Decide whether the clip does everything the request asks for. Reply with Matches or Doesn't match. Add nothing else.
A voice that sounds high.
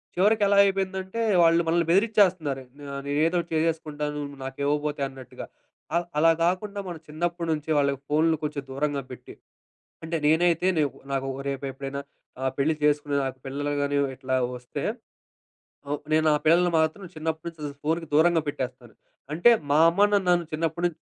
Doesn't match